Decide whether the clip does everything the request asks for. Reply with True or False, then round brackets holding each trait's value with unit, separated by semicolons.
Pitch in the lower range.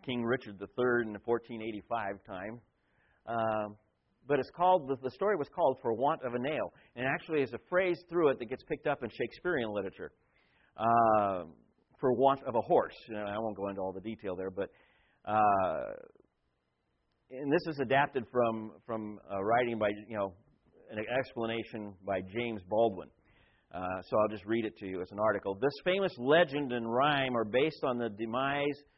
True (115 Hz)